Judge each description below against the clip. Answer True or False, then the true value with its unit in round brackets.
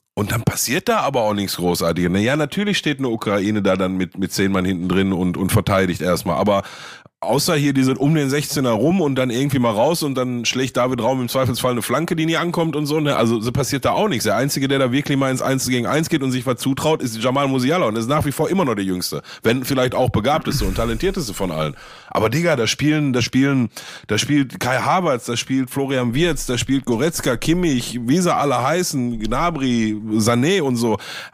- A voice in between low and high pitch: False (130 Hz)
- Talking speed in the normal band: False (230 wpm)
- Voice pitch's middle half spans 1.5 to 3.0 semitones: False (4.4 semitones)